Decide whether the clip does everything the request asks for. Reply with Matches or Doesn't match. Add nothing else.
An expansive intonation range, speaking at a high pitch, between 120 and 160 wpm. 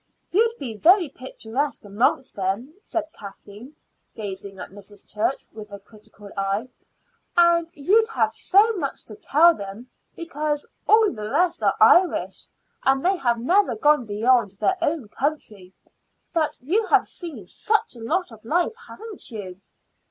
Matches